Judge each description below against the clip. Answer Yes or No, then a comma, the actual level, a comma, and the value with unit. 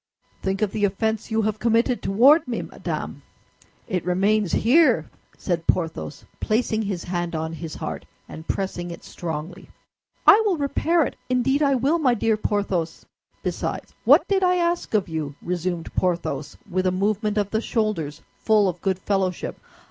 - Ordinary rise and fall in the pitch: Yes, average, 4.9 semitones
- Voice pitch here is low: No, high, 205 Hz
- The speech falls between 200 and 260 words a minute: No, average, 165 wpm